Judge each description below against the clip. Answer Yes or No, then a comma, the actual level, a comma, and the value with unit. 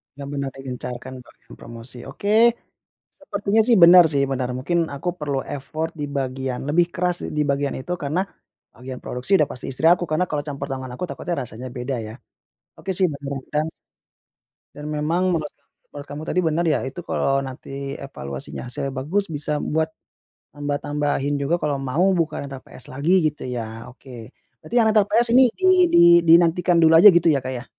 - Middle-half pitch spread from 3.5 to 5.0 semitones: Yes, average, 4.4 semitones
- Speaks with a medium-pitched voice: Yes, medium, 145 Hz